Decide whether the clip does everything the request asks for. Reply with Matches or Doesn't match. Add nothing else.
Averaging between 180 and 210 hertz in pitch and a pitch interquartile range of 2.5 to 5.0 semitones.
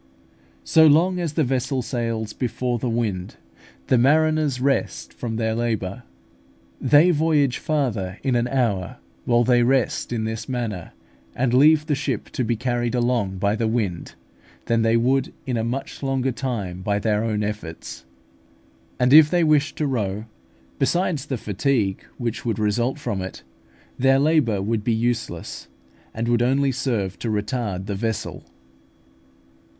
Doesn't match